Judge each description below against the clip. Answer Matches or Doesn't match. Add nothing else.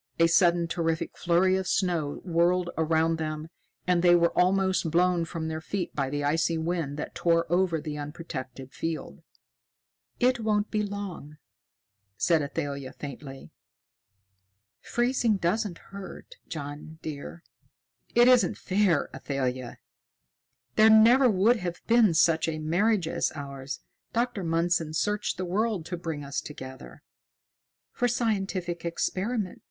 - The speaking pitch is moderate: Matches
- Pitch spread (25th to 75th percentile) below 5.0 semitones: Matches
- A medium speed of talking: Doesn't match